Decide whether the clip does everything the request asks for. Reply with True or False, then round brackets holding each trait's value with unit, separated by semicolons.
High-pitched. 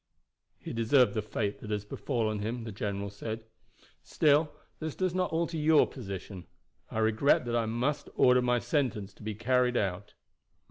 False (115 Hz)